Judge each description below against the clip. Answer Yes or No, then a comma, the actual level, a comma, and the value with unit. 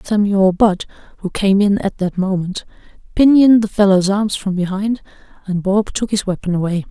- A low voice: No, high, 200 Hz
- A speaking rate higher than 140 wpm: Yes, average, 175 wpm